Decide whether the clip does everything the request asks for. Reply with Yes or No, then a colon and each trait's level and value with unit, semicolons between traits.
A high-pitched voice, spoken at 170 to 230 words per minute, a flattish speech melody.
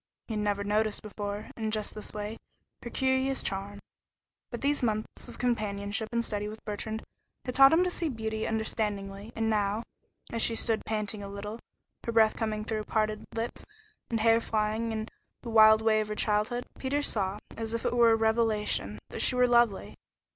Yes: high, 220 Hz; average, 190 wpm; narrow, 1.6 semitones